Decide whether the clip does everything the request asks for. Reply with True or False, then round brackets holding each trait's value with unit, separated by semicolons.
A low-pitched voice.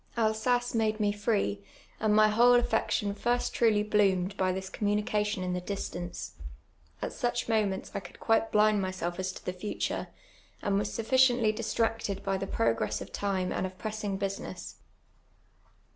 False (210 Hz)